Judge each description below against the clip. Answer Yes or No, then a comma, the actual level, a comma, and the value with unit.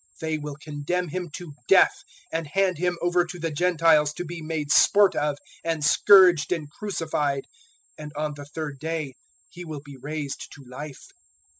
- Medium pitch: Yes, medium, 155 Hz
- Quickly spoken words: No, average, 175 wpm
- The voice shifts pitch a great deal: No, average, 3.1 semitones